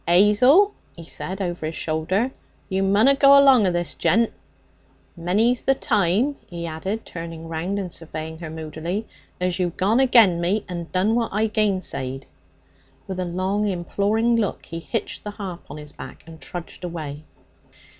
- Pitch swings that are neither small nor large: Yes, average, 4.3 semitones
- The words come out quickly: No, average, 165 wpm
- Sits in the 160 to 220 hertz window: Yes, medium, 185 Hz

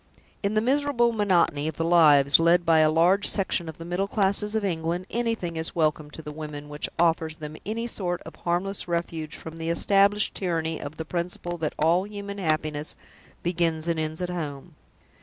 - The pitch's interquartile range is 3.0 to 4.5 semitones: Yes, average, 3.7 semitones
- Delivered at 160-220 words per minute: Yes, average, 190 wpm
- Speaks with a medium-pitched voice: Yes, medium, 170 Hz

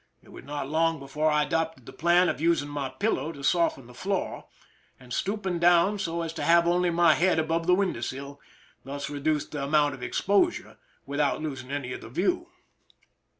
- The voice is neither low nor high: Yes, medium, 160 Hz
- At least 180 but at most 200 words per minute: Yes, average, 195 wpm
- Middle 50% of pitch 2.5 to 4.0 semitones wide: Yes, average, 3.5 semitones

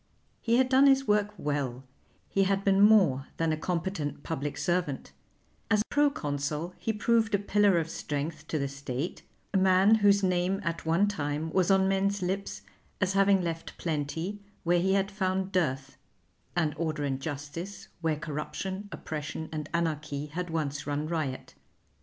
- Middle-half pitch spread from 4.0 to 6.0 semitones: Yes, average, 4.7 semitones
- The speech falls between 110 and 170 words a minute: Yes, average, 165 wpm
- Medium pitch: Yes, medium, 170 Hz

